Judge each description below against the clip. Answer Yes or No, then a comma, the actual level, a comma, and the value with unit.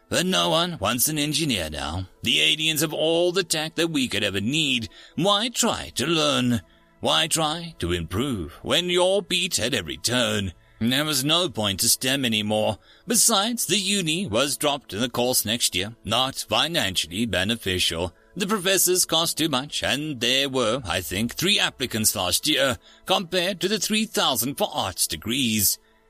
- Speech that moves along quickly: No, average, 170 wpm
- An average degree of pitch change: No, wide, 8.0 semitones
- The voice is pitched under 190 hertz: Yes, low, 135 Hz